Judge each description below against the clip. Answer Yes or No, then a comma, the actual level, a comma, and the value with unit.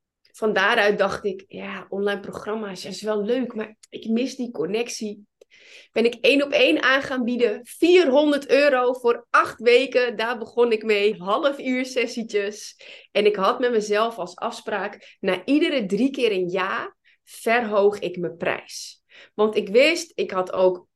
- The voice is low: No, high, 230 Hz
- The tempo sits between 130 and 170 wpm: Yes, average, 165 wpm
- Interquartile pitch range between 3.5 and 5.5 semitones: Yes, average, 3.9 semitones